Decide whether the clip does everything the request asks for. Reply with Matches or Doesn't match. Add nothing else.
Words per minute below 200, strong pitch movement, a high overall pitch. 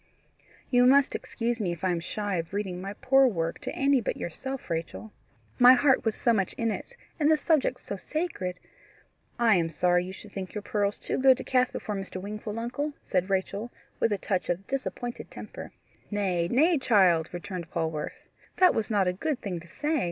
Doesn't match